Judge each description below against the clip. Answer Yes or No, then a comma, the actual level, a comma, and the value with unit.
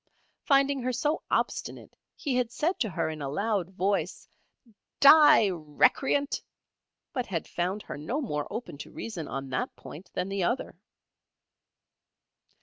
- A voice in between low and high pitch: No, high, 205 Hz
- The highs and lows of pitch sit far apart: Yes, wide, 8.2 semitones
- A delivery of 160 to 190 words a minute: No, average, 145 wpm